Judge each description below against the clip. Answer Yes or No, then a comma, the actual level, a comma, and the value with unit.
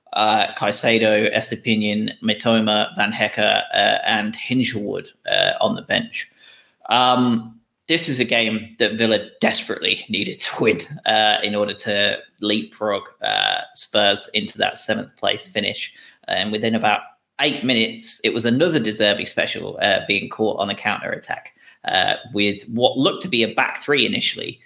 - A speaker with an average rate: Yes, average, 150 wpm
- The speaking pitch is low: Yes, low, 110 Hz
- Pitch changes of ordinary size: No, narrow, 1.6 semitones